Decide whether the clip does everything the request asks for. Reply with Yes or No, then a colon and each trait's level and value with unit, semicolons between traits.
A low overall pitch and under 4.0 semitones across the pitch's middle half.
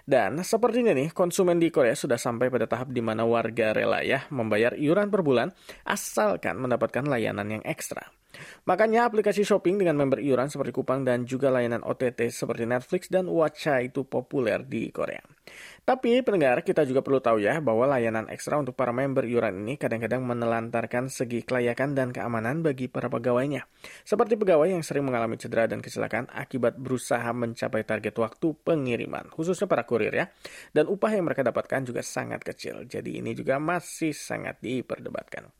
No: low, 130 Hz; average, 5.3 semitones